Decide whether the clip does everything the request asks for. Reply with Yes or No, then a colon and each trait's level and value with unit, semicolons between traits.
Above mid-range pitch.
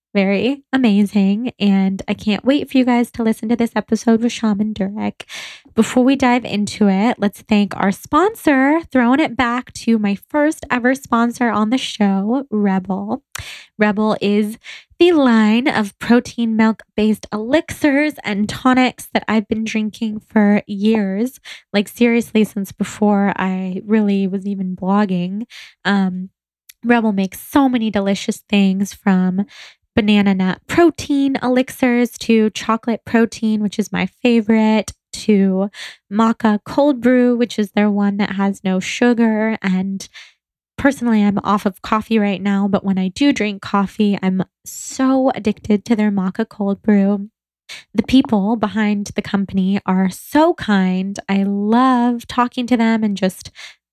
Yes: high, 215 Hz